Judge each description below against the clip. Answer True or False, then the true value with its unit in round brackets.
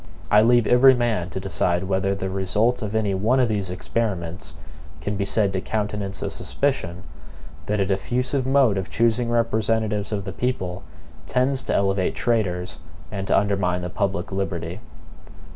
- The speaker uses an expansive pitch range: False (3.5 semitones)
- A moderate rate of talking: True (160 wpm)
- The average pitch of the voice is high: False (100 Hz)